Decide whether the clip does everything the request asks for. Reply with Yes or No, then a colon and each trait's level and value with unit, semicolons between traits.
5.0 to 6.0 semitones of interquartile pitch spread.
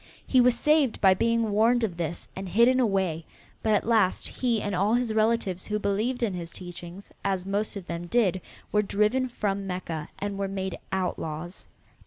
No: average, 3.8 semitones